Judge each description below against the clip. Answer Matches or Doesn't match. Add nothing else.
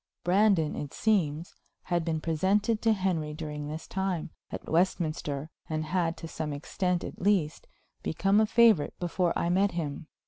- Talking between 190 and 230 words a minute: Doesn't match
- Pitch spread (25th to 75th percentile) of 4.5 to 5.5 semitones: Doesn't match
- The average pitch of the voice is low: Doesn't match